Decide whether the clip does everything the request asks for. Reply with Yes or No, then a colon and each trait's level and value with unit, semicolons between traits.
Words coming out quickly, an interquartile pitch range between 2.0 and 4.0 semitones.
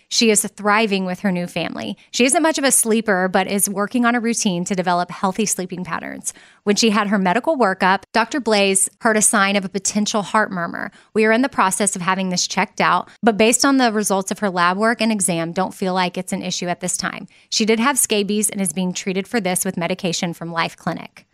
Yes: fast, 240 wpm; average, 3.3 semitones